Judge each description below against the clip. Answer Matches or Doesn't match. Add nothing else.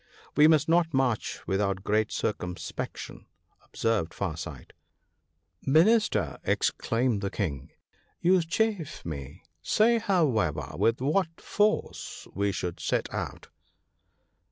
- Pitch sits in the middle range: Doesn't match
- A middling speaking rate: Doesn't match